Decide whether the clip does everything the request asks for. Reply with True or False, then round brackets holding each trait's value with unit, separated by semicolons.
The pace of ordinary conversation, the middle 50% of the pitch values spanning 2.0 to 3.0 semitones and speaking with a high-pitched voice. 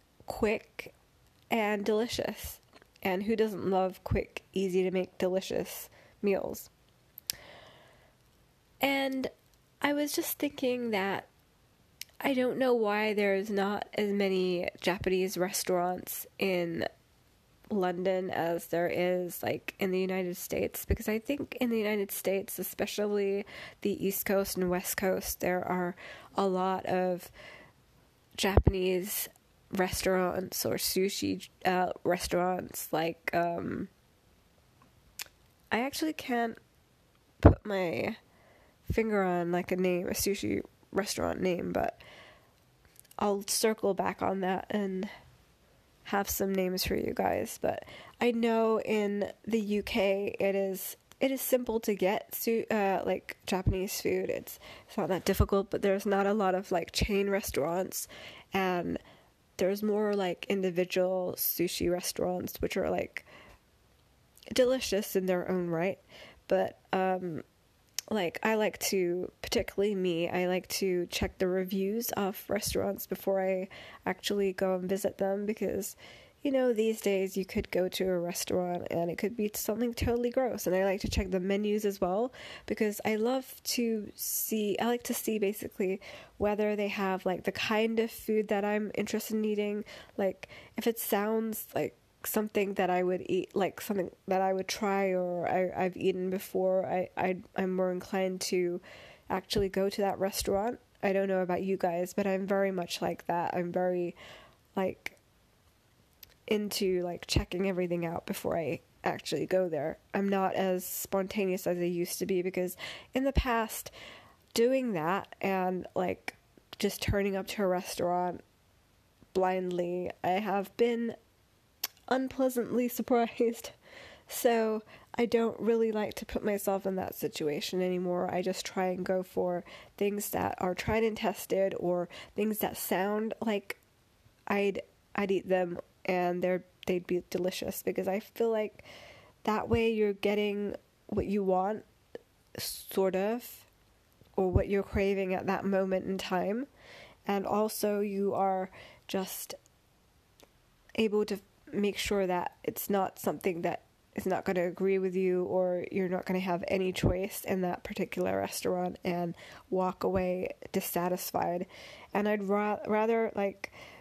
True (145 wpm; 2.4 semitones; 195 Hz)